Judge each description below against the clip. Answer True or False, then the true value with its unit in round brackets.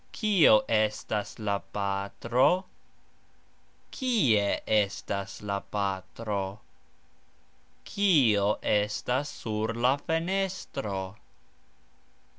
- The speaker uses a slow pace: True (65 wpm)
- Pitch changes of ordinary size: False (6.0 semitones)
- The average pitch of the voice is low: True (110 Hz)